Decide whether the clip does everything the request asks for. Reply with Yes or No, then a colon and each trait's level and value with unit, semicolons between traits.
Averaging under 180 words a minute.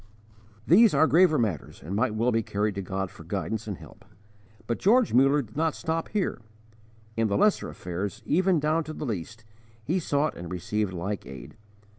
No: average, 185 wpm